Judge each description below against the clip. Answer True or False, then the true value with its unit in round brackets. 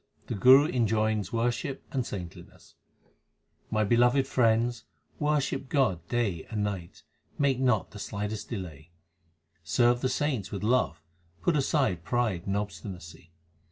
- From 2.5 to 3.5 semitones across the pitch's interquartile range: False (4.8 semitones)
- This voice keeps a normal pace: False (125 wpm)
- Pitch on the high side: False (110 Hz)